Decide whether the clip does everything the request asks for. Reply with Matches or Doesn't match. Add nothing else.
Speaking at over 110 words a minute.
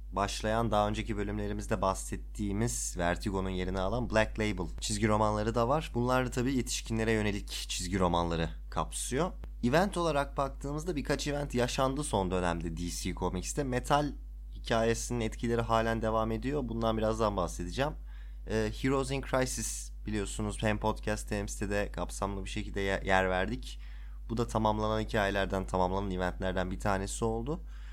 Matches